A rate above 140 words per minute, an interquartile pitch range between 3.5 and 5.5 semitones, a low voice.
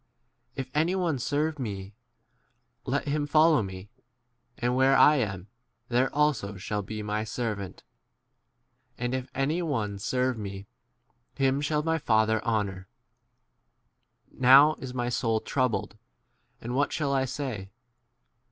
No: slow, 135 wpm; average, 5.1 semitones; low, 125 Hz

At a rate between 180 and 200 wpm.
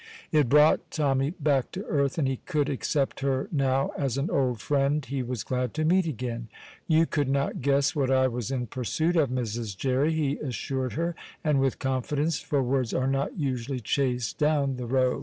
Yes: average, 195 wpm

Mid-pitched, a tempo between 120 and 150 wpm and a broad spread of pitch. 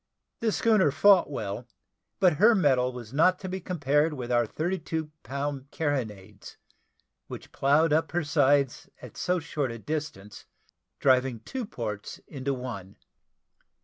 No: medium, 145 Hz; average, 145 wpm; average, 4.8 semitones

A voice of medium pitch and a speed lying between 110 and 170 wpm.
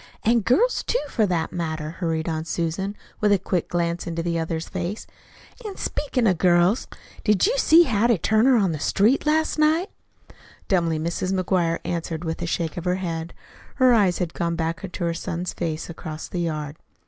No: medium, 175 Hz; average, 185 wpm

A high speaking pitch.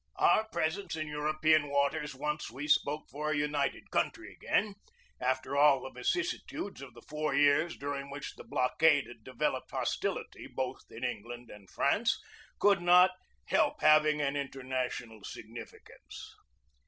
No: medium, 145 Hz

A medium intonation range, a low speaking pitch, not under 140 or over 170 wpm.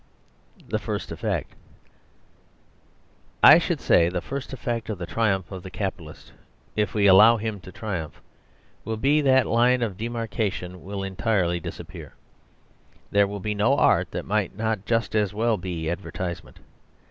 Yes: average, 3.5 semitones; low, 105 Hz; average, 155 wpm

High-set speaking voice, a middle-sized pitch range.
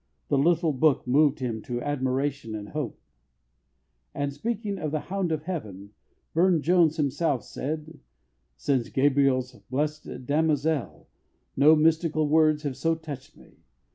No: medium, 150 Hz; average, 3.4 semitones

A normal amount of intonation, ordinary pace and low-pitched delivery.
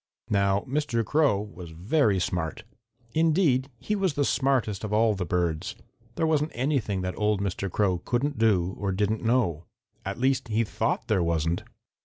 No: wide, 5.9 semitones; average, 165 wpm; low, 105 Hz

